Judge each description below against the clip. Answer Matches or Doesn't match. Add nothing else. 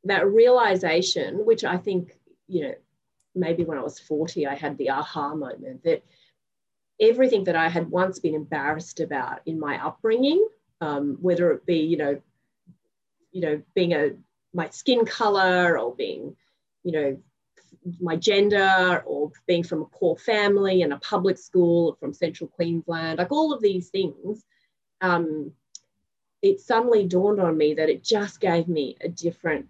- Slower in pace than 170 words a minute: Matches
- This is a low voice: Doesn't match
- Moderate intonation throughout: Matches